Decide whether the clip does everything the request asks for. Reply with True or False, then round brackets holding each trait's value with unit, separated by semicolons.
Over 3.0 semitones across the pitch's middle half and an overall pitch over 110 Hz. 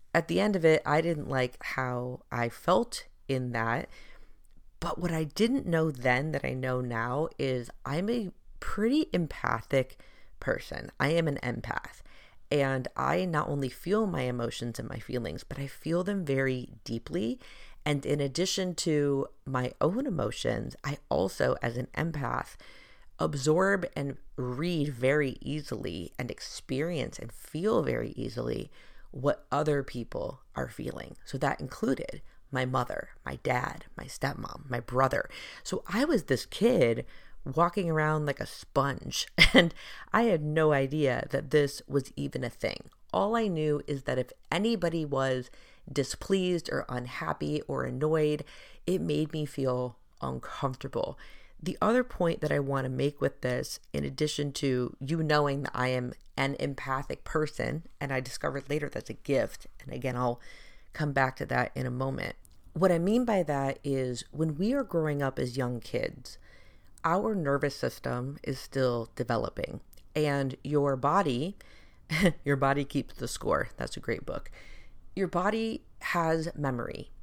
True (4.0 semitones; 140 Hz)